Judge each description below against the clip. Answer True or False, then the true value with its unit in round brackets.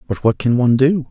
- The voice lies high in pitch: False (125 Hz)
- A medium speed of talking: False (270 wpm)